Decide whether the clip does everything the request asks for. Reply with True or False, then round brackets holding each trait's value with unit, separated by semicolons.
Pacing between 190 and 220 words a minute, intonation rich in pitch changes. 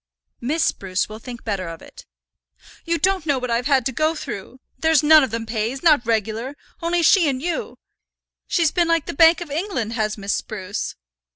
True (195 wpm; 6.7 semitones)